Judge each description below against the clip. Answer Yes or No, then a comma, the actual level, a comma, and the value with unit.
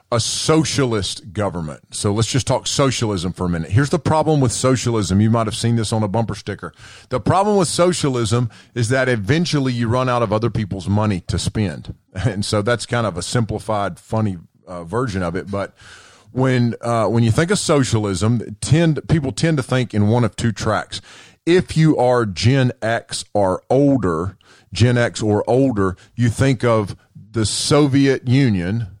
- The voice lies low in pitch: Yes, low, 115 Hz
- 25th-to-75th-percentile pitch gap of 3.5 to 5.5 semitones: Yes, average, 3.8 semitones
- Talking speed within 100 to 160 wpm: No, average, 180 wpm